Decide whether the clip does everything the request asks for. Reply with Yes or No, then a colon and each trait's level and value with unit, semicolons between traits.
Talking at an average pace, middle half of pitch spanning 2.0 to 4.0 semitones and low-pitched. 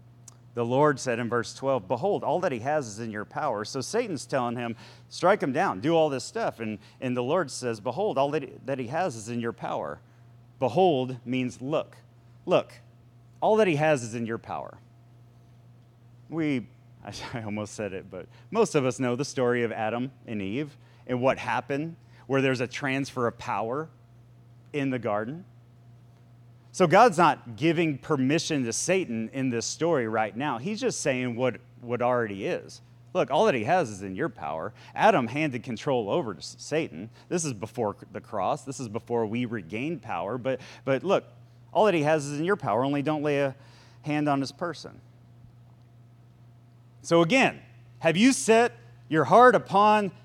Yes: average, 180 wpm; average, 3.5 semitones; low, 120 Hz